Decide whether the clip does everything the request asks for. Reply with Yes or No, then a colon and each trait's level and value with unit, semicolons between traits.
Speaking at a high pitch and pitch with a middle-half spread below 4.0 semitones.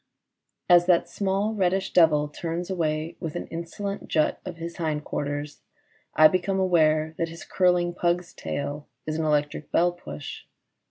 No: medium, 170 Hz; narrow, 2.6 semitones